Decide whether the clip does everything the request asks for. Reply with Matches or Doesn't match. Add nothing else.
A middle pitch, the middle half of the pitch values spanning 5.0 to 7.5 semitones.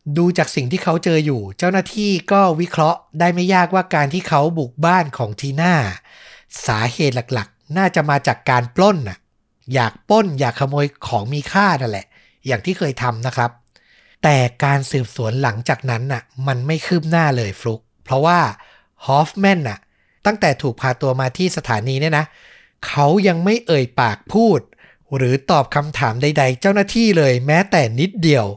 Matches